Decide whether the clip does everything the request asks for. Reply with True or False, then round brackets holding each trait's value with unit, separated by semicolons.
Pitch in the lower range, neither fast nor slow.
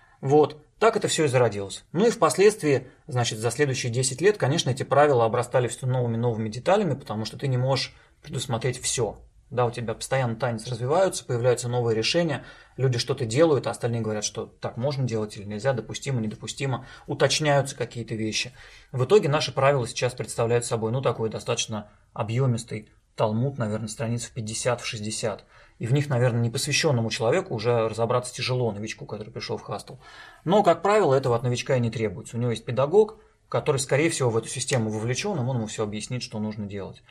False (125 Hz; 185 wpm)